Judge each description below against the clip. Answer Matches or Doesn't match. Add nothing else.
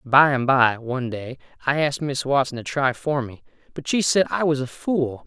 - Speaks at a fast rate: Matches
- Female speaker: Doesn't match